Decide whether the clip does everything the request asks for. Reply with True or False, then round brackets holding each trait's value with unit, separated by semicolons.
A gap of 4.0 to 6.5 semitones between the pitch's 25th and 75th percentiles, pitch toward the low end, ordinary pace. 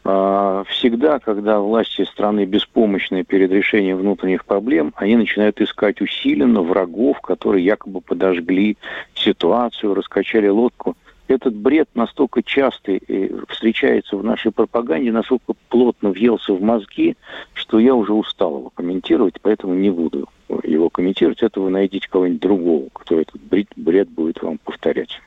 False (3.2 semitones; 105 Hz; 130 wpm)